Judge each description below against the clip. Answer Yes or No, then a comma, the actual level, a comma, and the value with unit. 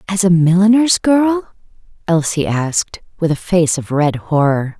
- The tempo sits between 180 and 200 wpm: No, average, 150 wpm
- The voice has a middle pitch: Yes, medium, 175 Hz